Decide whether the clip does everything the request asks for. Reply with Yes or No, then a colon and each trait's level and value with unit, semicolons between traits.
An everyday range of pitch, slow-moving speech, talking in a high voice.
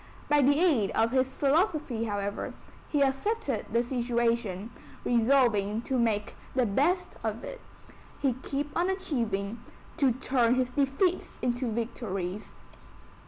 Yes: average, 3.9 semitones; slow, 125 wpm; very high, 250 Hz